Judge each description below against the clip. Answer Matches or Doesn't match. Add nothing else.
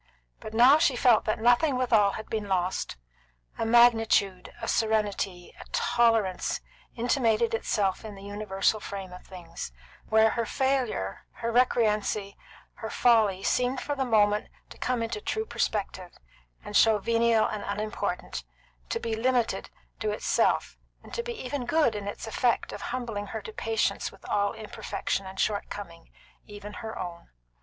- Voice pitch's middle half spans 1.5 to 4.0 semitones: Matches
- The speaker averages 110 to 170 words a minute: Matches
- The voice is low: Doesn't match